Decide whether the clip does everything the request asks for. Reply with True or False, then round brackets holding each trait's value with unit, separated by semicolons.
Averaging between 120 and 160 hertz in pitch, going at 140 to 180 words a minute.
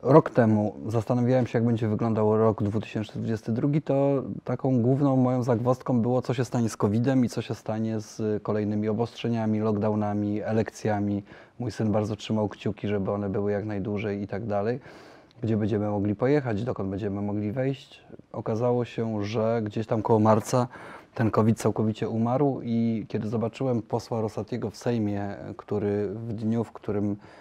False (110 Hz; 160 wpm)